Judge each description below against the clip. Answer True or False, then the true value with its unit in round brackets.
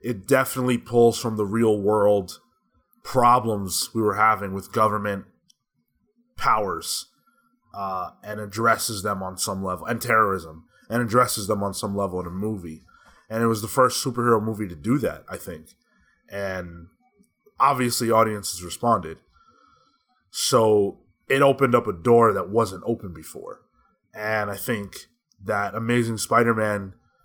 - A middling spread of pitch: True (3.3 semitones)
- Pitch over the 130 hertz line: False (110 Hz)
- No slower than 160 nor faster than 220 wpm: False (145 wpm)